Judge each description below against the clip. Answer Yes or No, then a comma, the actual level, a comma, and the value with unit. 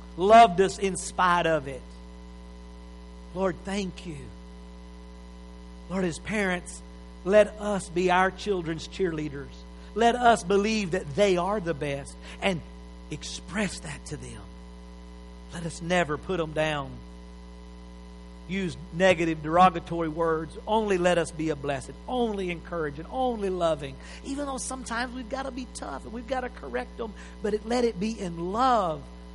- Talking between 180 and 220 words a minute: No, average, 145 wpm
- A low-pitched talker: No, medium, 170 Hz